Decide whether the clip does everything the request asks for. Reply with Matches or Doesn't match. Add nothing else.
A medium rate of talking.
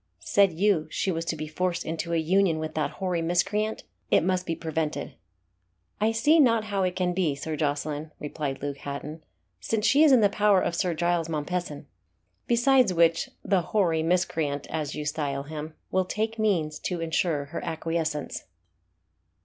Matches